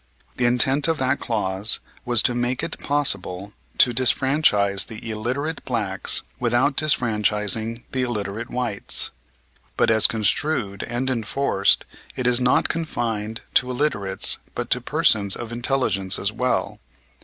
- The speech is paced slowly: Yes, slow, 130 wpm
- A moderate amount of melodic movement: Yes, average, 3.7 semitones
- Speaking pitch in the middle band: No, low, 120 Hz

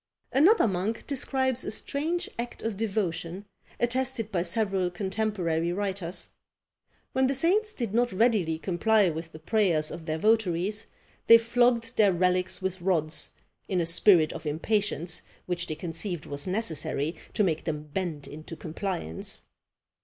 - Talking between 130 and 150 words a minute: Yes, average, 145 wpm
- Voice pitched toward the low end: No, high, 190 Hz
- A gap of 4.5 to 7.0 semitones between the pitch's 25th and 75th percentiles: Yes, average, 5.2 semitones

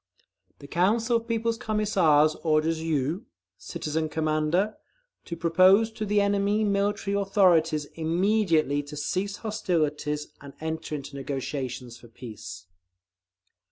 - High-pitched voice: No, medium, 165 Hz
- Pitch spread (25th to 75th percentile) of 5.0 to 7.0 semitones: Yes, average, 5.3 semitones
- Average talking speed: No, slow, 115 wpm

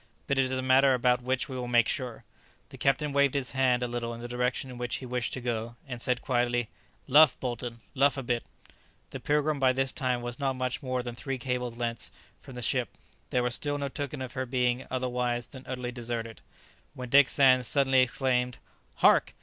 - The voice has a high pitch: No, low, 125 Hz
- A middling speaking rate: No, fast, 215 wpm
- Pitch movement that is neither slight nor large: No, narrow, 1.6 semitones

